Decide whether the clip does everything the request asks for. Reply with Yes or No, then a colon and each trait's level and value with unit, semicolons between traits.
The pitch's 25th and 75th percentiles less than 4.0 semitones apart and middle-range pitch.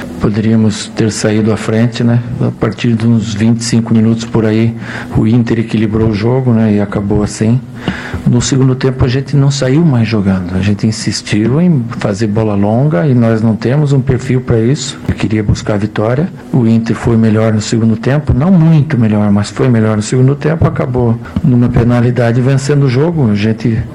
No: average, 2.8 semitones; low, 115 Hz